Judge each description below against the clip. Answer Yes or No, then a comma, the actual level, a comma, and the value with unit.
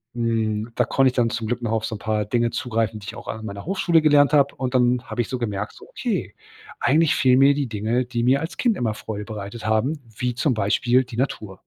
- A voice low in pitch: Yes, low, 120 Hz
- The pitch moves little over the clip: No, average, 3.3 semitones